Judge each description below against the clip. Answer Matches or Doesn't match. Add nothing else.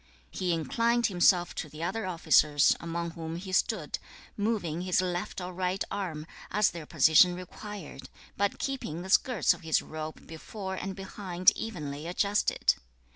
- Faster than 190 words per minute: Doesn't match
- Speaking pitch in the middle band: Matches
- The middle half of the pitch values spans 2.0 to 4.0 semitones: Matches